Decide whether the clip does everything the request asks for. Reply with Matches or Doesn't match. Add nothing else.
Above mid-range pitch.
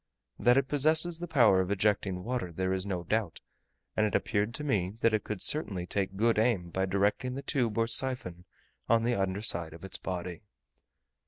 Doesn't match